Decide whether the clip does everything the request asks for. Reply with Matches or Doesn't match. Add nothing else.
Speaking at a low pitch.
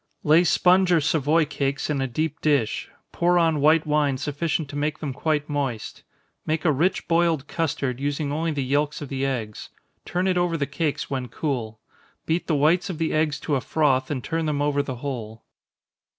Doesn't match